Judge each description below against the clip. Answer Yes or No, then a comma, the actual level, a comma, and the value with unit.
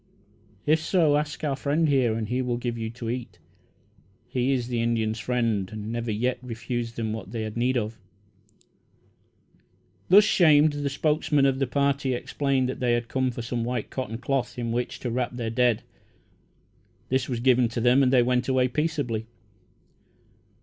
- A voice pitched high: No, low, 125 Hz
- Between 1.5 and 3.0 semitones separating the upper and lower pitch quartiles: Yes, average, 2.7 semitones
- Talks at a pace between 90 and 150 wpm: No, average, 175 wpm